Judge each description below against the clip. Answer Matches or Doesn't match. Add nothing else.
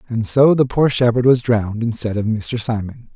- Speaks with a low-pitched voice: Matches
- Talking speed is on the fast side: Matches